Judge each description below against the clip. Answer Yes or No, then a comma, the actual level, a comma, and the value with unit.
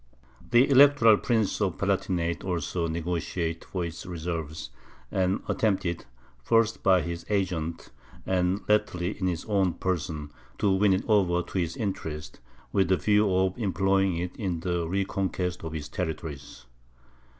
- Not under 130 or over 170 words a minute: Yes, average, 145 wpm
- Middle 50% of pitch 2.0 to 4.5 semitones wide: Yes, average, 2.7 semitones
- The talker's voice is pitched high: No, very low, 90 Hz